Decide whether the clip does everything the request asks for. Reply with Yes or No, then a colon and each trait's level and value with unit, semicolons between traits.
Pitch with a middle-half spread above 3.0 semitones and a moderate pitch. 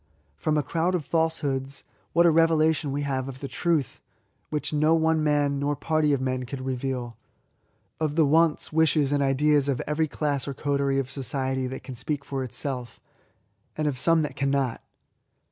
No: average, 2.7 semitones; medium, 145 Hz